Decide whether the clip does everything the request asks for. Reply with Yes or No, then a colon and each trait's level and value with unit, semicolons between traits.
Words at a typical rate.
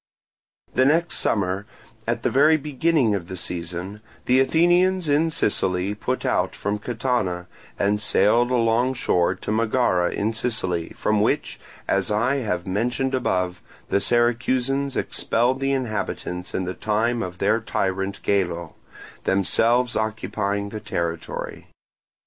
No: slow, 130 wpm